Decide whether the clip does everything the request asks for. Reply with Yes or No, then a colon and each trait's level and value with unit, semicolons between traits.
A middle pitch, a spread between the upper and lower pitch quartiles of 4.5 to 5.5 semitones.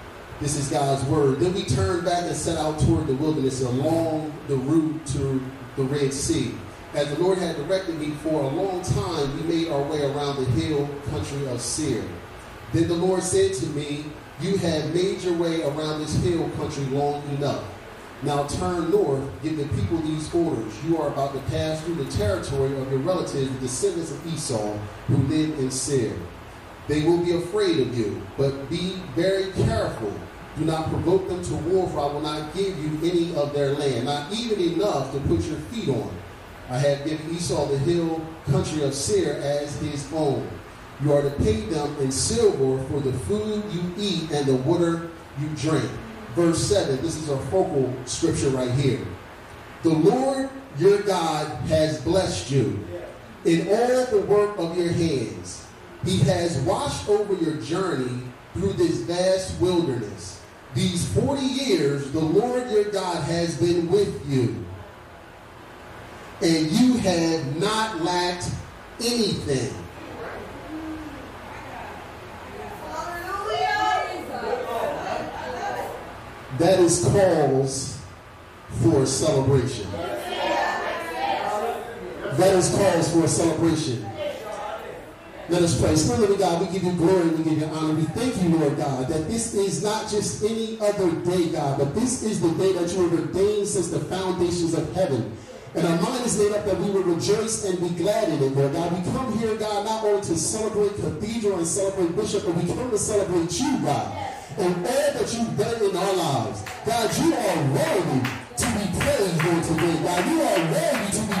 Yes: medium, 160 Hz; average, 5.2 semitones